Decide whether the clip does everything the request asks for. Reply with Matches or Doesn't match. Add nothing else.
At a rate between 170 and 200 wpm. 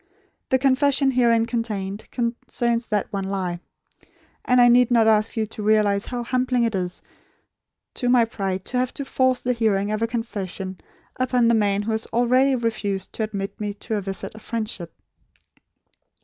Matches